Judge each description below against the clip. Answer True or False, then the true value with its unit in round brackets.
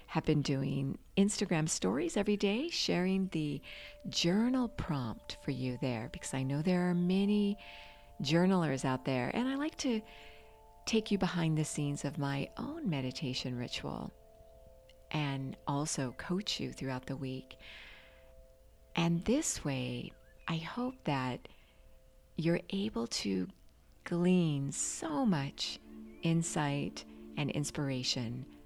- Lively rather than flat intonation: True (6.5 semitones)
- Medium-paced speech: False (125 wpm)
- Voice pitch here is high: False (145 Hz)